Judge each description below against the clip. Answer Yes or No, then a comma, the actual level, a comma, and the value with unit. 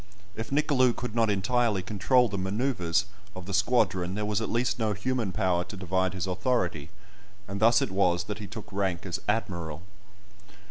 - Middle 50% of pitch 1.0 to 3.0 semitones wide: No, average, 3.7 semitones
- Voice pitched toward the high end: No, low, 100 Hz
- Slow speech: No, average, 180 wpm